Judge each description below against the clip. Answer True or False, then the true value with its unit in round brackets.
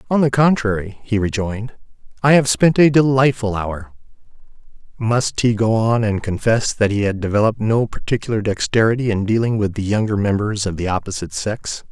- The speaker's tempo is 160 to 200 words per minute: True (170 wpm)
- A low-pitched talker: True (110 Hz)